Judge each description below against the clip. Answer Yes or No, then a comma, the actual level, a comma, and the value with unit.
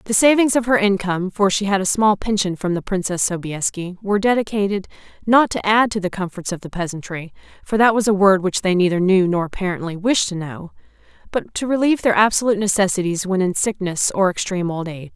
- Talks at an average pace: No, fast, 210 wpm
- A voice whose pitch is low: No, high, 195 Hz